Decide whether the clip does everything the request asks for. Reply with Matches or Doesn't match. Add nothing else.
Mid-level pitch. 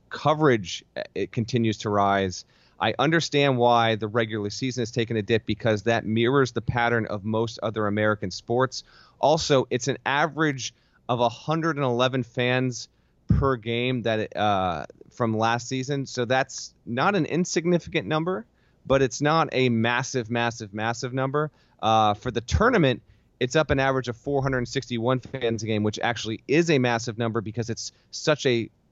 Doesn't match